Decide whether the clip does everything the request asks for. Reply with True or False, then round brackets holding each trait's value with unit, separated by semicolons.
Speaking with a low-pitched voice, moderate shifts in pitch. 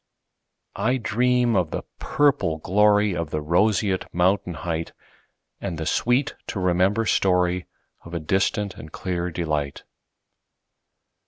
True (95 Hz; 3.7 semitones)